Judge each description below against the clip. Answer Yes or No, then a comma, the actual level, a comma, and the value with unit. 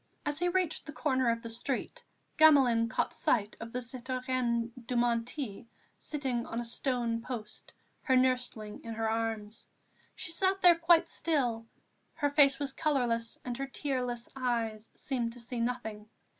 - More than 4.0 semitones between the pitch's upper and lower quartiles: No, average, 3.4 semitones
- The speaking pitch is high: Yes, very high, 250 Hz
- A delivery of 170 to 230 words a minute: No, average, 155 wpm